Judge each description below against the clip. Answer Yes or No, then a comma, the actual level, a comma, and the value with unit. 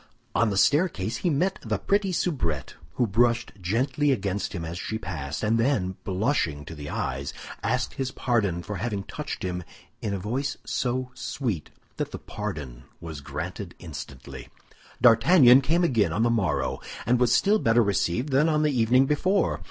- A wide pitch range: Yes, wide, 6.7 semitones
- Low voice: Yes, low, 115 Hz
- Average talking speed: Yes, average, 170 wpm